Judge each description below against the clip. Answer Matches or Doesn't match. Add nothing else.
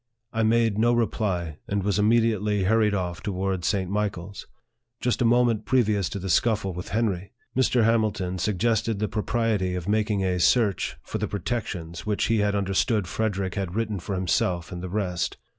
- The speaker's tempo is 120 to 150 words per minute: Doesn't match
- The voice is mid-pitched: Doesn't match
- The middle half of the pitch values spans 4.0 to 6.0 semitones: Doesn't match